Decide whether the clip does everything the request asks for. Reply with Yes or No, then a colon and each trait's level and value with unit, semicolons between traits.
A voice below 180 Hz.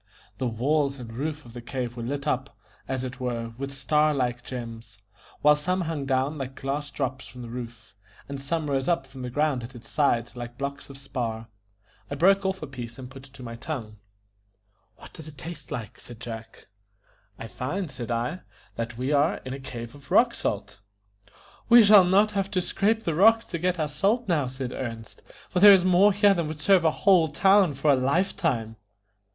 Yes: medium, 140 Hz